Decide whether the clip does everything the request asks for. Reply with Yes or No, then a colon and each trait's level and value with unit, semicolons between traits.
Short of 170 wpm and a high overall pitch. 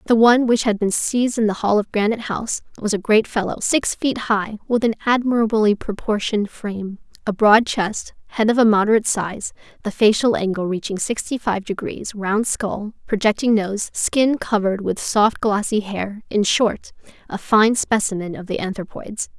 No: average, 175 wpm; high, 215 Hz